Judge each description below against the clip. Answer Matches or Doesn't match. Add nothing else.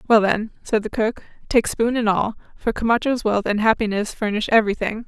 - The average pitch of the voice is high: Matches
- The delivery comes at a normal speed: Matches